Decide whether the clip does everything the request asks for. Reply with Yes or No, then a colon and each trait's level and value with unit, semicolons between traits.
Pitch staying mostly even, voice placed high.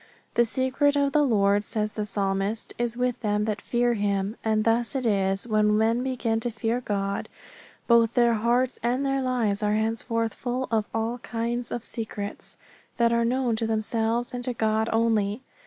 Yes: narrow, 2.3 semitones; high, 230 Hz